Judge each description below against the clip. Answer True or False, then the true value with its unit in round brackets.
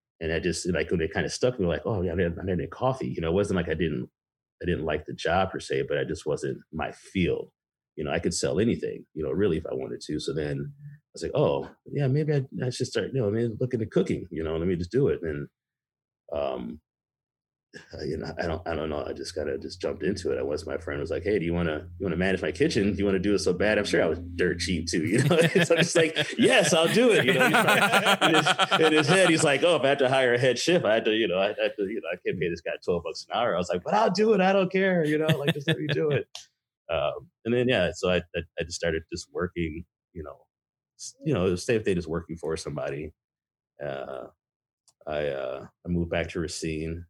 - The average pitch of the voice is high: False (135 Hz)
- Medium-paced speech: False (285 wpm)